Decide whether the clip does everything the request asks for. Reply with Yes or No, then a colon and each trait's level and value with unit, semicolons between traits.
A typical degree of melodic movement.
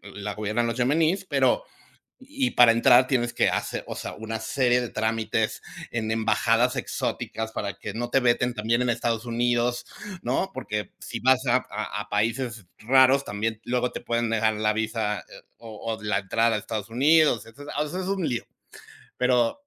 No: narrow, 2.3 semitones